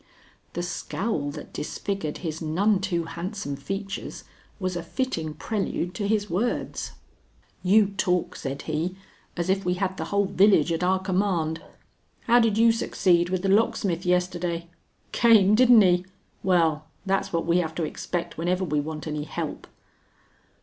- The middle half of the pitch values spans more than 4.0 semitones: No, average, 3.3 semitones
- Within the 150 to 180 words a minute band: Yes, average, 155 wpm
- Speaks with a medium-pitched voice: Yes, medium, 180 Hz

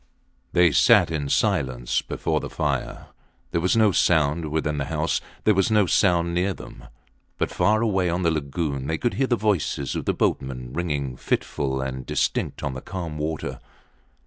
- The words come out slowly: No, average, 175 wpm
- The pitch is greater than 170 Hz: No, very low, 80 Hz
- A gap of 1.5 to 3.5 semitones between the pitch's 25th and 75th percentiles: No, average, 4.7 semitones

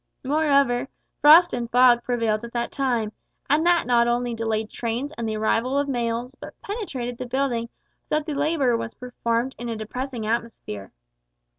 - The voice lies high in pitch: Yes, high, 245 Hz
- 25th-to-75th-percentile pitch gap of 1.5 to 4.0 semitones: Yes, average, 3.0 semitones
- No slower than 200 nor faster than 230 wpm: No, average, 170 wpm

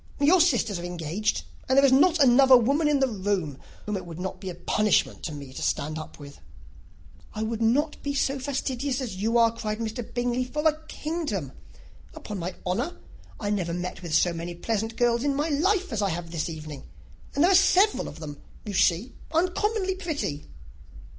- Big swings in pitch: Yes, wide, 8.2 semitones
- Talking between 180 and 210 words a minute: Yes, average, 195 wpm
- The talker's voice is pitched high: Yes, high, 225 Hz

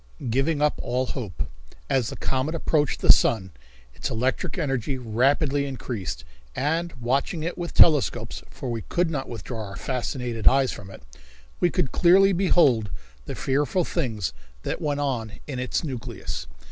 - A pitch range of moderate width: Yes, average, 4.3 semitones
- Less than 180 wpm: Yes, average, 155 wpm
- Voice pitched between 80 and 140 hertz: Yes, low, 135 Hz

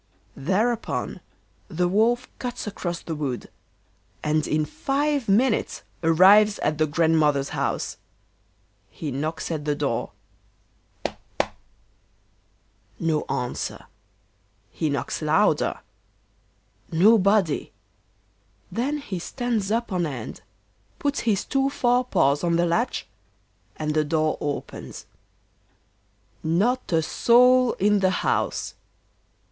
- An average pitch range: No, wide, 7.2 semitones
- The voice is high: No, medium, 180 Hz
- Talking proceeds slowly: Yes, slow, 110 wpm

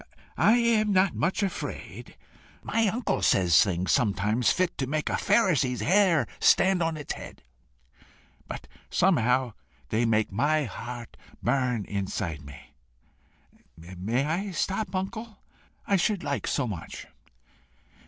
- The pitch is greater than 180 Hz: No, medium, 140 Hz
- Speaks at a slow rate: Yes, slow, 125 wpm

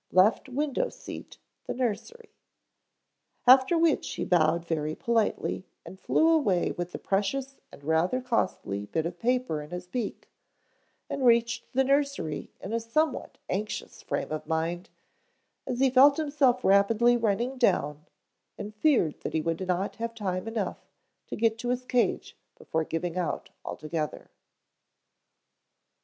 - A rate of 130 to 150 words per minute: Yes, average, 145 wpm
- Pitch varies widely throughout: Yes, wide, 6.6 semitones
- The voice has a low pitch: No, high, 220 Hz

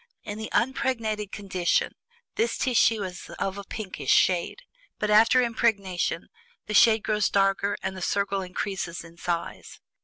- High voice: Yes, high, 200 Hz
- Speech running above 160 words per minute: No, average, 145 wpm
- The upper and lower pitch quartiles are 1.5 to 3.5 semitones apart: Yes, average, 2.9 semitones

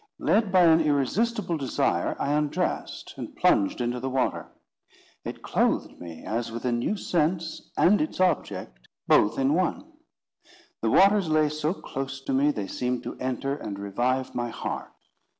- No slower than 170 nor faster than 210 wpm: No, average, 160 wpm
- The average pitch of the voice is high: No, medium, 140 Hz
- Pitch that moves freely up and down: Yes, wide, 5.8 semitones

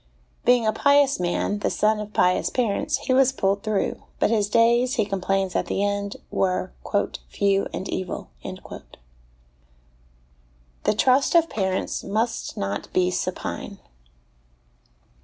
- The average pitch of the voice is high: Yes, high, 195 Hz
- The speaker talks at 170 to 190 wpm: No, slow, 135 wpm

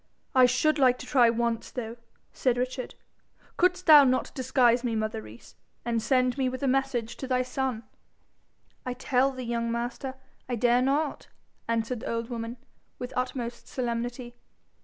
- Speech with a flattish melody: Yes, narrow, 1.9 semitones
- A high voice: Yes, very high, 250 Hz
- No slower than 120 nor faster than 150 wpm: No, average, 160 wpm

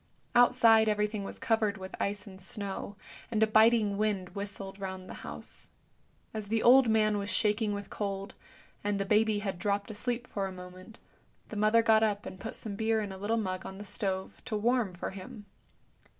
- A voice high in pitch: Yes, high, 205 Hz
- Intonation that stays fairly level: Yes, narrow, 2.0 semitones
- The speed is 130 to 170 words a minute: No, average, 195 wpm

